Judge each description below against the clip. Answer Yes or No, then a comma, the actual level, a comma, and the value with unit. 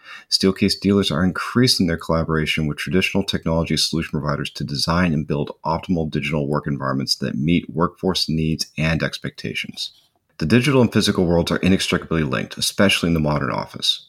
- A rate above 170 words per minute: No, average, 160 wpm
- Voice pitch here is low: Yes, very low, 80 Hz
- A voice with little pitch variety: No, average, 4.0 semitones